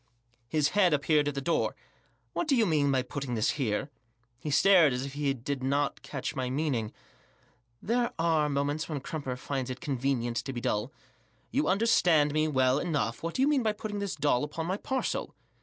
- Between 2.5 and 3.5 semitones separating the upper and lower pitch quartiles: No, average, 4.2 semitones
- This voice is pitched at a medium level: Yes, medium, 145 Hz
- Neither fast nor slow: Yes, average, 195 wpm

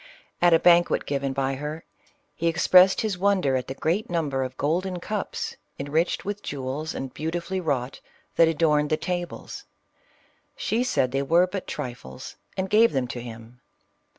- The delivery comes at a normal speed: Yes, average, 165 wpm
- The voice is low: No, medium, 160 Hz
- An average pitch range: Yes, average, 5.0 semitones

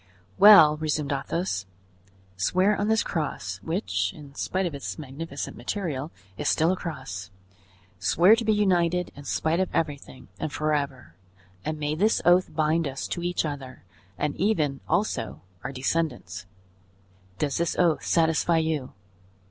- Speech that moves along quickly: No, average, 145 wpm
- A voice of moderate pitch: Yes, medium, 155 Hz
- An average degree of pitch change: Yes, average, 4.1 semitones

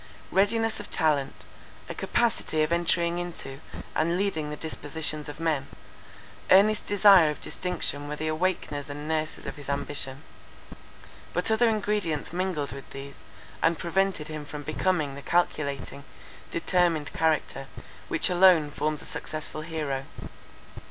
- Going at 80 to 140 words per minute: Yes, slow, 135 wpm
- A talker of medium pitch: Yes, medium, 155 Hz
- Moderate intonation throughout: Yes, average, 3.5 semitones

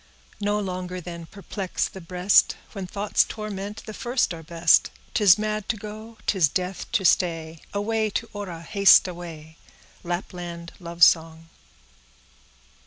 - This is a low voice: No, medium, 185 Hz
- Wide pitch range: No, average, 3.5 semitones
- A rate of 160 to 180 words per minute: No, slow, 135 wpm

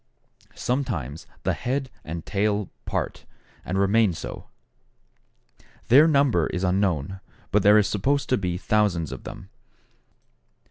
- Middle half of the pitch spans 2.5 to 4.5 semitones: No, wide, 5.4 semitones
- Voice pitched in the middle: No, low, 100 Hz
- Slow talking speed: Yes, slow, 125 wpm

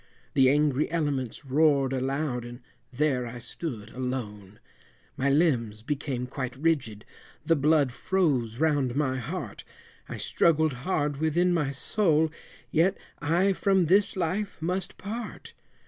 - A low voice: No, medium, 145 Hz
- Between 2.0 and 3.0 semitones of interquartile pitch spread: No, average, 4.4 semitones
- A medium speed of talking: No, slow, 130 wpm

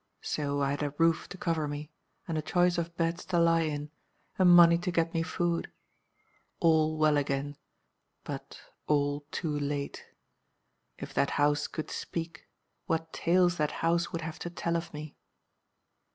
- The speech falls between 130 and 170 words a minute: Yes, average, 165 wpm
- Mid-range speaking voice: Yes, medium, 160 Hz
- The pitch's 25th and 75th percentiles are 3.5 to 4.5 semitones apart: No, narrow, 2.4 semitones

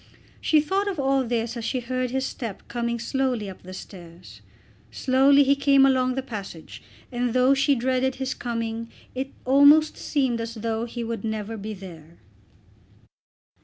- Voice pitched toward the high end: Yes, high, 245 Hz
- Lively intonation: No, average, 3.0 semitones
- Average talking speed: Yes, average, 165 wpm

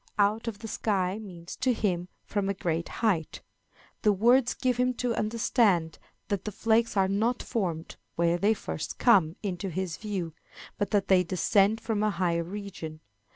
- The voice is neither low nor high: No, high, 200 Hz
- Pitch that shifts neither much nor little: Yes, average, 3.8 semitones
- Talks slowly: No, average, 170 wpm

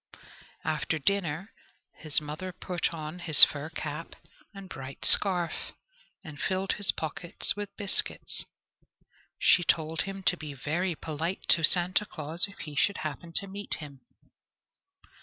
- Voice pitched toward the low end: No, medium, 165 Hz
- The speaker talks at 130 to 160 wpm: Yes, average, 140 wpm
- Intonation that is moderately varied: Yes, average, 3.7 semitones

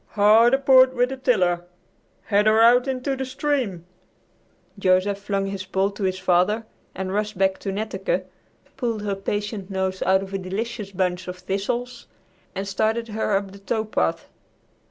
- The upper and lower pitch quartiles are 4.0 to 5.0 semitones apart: No, average, 3.2 semitones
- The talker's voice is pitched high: Yes, high, 200 Hz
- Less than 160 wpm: No, average, 165 wpm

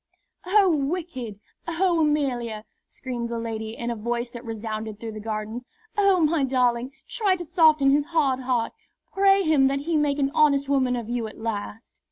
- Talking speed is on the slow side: No, average, 180 wpm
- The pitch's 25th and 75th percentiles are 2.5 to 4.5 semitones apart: No, average, 5.3 semitones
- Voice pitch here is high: Yes, very high, 260 Hz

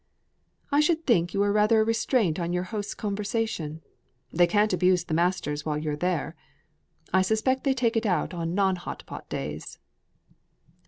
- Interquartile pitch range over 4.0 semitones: Yes, average, 4.4 semitones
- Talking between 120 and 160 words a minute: No, average, 170 wpm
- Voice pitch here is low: No, high, 190 Hz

